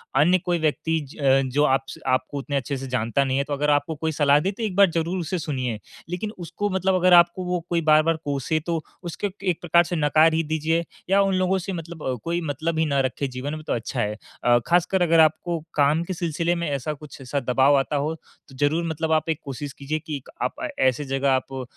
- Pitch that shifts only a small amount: No, average, 3.6 semitones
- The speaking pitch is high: No, medium, 155 Hz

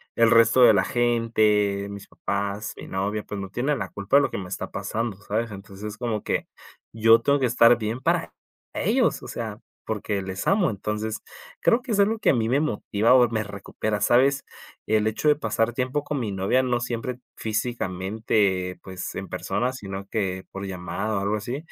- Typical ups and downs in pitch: Yes, average, 3.5 semitones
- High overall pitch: No, low, 110 Hz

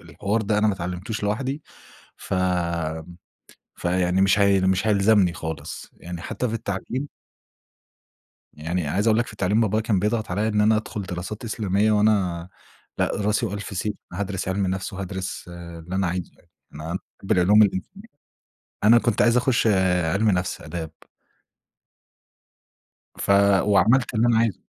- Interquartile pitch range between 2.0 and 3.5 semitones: Yes, average, 3.2 semitones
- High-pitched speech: No, low, 100 Hz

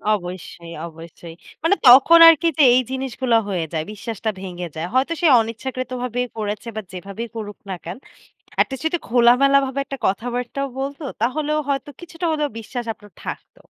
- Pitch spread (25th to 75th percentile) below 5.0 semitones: No, wide, 5.5 semitones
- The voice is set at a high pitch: Yes, high, 245 Hz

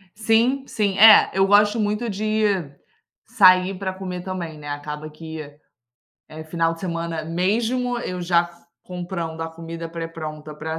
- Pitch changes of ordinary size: Yes, average, 4.0 semitones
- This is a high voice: No, medium, 180 Hz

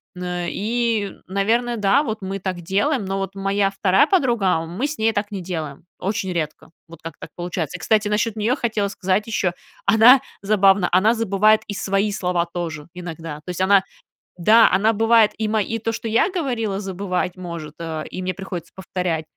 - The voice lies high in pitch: Yes, high, 195 Hz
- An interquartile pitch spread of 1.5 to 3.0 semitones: No, average, 3.5 semitones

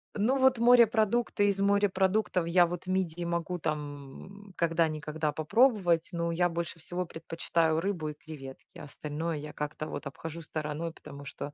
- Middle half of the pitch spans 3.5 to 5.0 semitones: Yes, average, 4.0 semitones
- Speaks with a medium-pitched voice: Yes, medium, 170 Hz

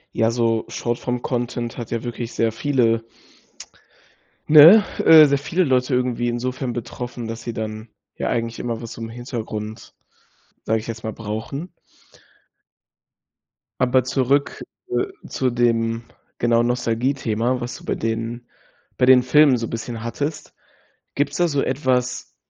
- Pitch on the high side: No, low, 120 Hz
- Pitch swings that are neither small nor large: No, narrow, 2.3 semitones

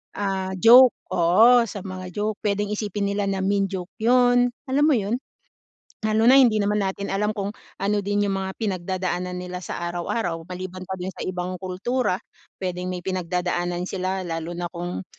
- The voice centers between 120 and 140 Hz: No, high, 190 Hz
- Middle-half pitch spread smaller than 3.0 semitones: Yes, narrow, 2.5 semitones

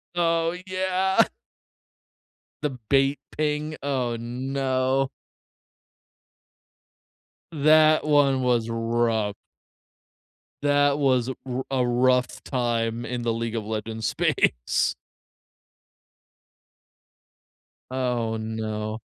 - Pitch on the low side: Yes, low, 130 Hz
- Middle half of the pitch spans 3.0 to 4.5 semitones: Yes, average, 3.8 semitones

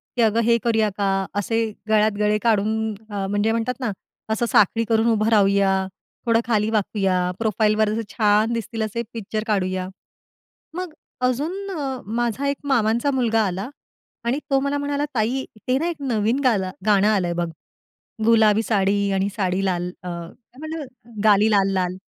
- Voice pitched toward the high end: Yes, high, 220 Hz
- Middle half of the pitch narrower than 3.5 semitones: Yes, average, 2.9 semitones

